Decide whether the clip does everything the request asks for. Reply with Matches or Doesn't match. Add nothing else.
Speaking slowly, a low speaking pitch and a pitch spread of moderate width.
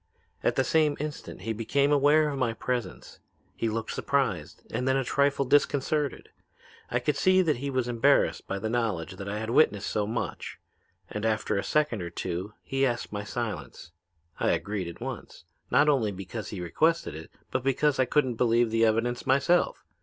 Doesn't match